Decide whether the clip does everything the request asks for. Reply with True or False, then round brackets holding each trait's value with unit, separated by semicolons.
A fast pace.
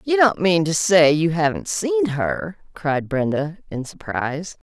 False (165 wpm)